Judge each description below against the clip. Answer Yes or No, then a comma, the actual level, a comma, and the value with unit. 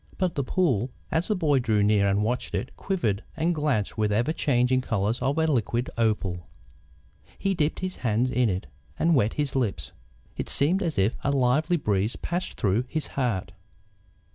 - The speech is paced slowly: No, average, 185 wpm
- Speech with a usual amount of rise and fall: No, wide, 6.6 semitones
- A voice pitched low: Yes, low, 125 Hz